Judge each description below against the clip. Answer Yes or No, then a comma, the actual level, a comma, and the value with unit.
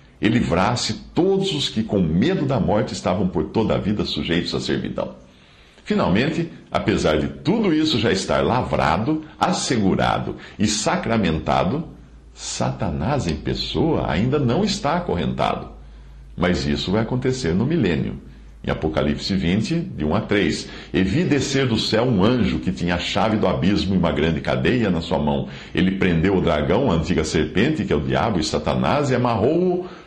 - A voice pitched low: Yes, very low, 85 Hz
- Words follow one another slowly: No, average, 165 wpm